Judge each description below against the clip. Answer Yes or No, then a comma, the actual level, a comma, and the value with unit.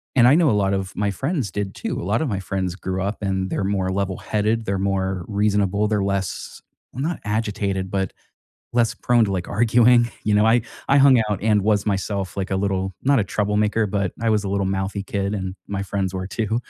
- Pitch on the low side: Yes, low, 100 Hz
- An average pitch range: No, narrow, 2.2 semitones